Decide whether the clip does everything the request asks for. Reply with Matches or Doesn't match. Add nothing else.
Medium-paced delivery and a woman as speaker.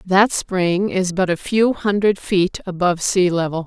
Matches